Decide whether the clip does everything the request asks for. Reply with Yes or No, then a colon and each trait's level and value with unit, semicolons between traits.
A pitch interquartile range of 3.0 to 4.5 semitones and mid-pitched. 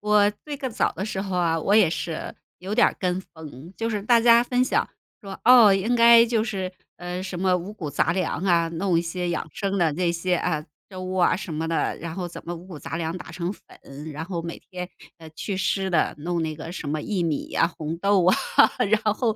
Yes: average, 3.4 semitones; medium, 180 Hz